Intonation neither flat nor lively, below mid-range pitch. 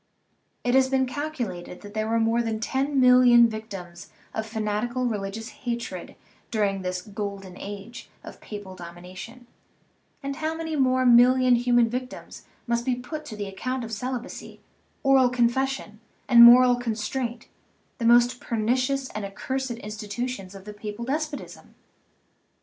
No: average, 3.4 semitones; high, 235 Hz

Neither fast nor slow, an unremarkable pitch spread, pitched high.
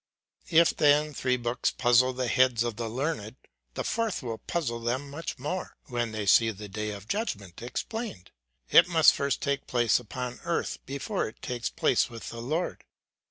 No: average, 175 wpm; average, 4.2 semitones; low, 125 Hz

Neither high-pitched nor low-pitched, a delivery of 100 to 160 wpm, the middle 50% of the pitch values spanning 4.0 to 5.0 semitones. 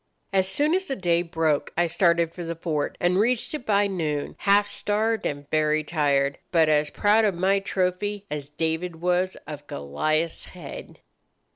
No: medium, 175 Hz; average, 170 wpm; average, 4.3 semitones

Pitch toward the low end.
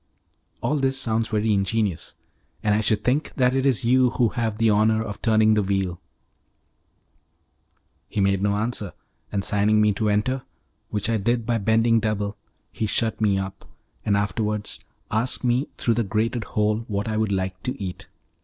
Yes: low, 110 Hz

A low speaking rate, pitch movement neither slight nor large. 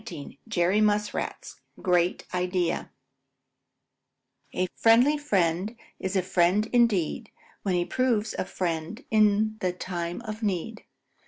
Yes: slow, 115 wpm; average, 3.6 semitones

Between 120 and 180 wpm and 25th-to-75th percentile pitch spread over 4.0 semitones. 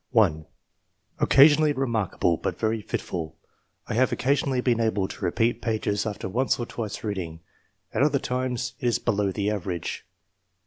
Yes: average, 150 wpm; average, 4.6 semitones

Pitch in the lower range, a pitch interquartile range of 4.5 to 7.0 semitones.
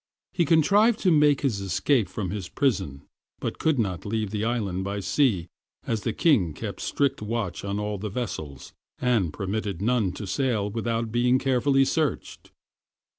Yes: low, 110 Hz; average, 5.1 semitones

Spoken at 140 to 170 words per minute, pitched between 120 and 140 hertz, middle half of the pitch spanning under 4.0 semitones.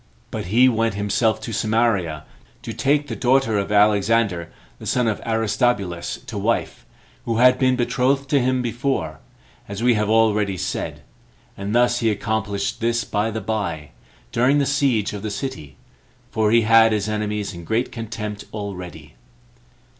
No: average, 160 wpm; low, 110 Hz; average, 3.0 semitones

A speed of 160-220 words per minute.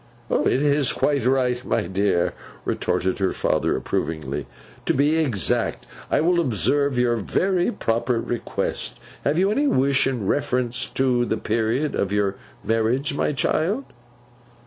No: average, 140 wpm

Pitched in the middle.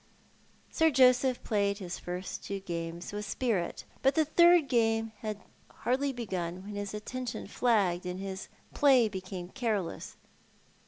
No: high, 210 Hz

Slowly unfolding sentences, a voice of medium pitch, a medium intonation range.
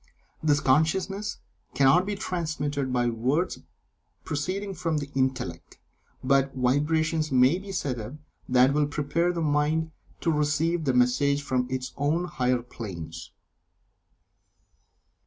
Yes: slow, 120 wpm; medium, 145 Hz; average, 4.0 semitones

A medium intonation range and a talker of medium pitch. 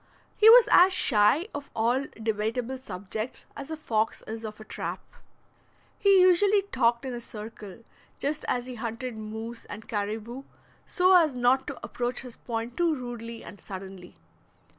No: average, 4.4 semitones; high, 240 Hz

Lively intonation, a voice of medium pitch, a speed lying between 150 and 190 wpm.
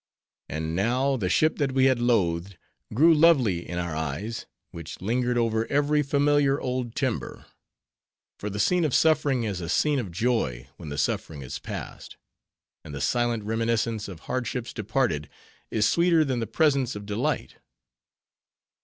No: wide, 6.2 semitones; low, 115 Hz; average, 155 wpm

